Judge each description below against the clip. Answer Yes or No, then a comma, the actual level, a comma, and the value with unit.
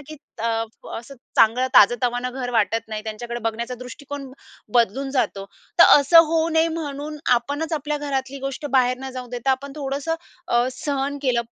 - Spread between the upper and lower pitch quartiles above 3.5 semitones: No, average, 3.2 semitones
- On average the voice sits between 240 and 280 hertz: Yes, very high, 260 Hz